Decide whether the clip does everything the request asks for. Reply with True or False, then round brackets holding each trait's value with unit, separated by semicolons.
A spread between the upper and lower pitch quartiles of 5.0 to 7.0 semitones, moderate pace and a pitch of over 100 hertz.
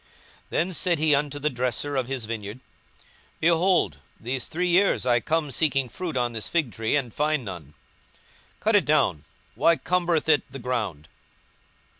True (5.4 semitones; 165 wpm; 135 Hz)